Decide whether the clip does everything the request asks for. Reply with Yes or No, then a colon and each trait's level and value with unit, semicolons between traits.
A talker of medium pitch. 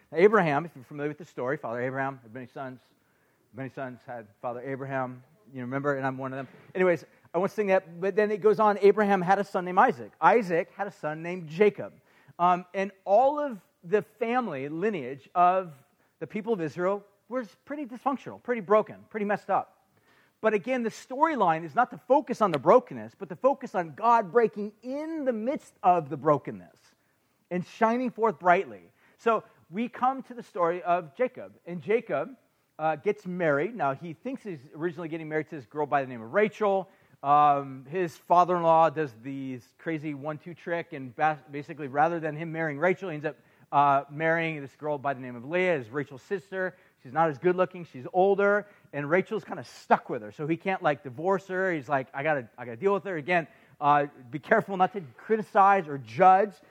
Yes: medium, 175 Hz